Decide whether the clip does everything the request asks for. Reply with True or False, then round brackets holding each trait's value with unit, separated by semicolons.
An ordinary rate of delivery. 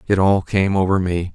False (225 wpm)